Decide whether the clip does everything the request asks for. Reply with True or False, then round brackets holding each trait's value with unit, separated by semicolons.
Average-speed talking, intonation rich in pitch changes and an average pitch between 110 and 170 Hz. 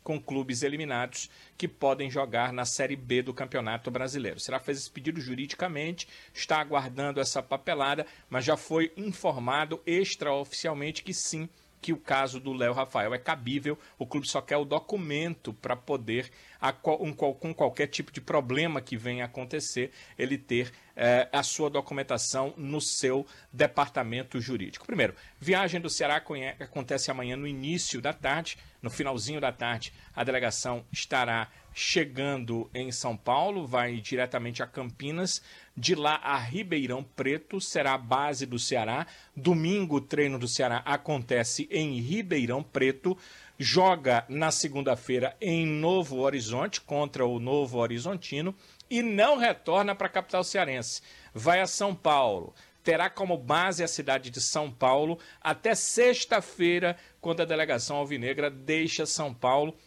False (145 wpm; 4.1 semitones; 140 Hz)